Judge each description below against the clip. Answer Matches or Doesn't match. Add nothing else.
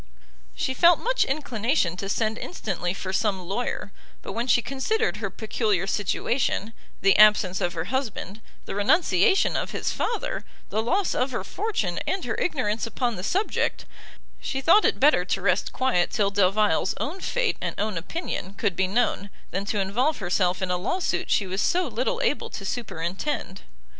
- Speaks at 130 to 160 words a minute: Doesn't match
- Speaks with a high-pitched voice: Matches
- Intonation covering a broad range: Matches